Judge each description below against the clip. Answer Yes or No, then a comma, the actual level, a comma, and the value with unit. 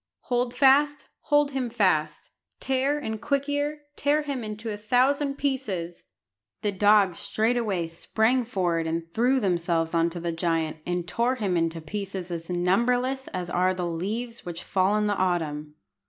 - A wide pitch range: Yes, wide, 6.6 semitones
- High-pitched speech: Yes, high, 205 Hz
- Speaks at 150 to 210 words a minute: Yes, average, 155 wpm